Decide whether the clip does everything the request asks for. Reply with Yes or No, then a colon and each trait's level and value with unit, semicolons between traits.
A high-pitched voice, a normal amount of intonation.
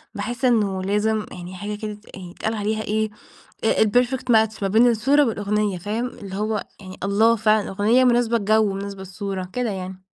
No: high, 210 Hz; narrow, 2.2 semitones